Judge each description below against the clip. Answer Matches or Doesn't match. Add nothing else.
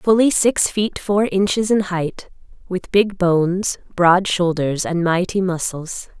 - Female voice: Matches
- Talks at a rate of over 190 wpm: Doesn't match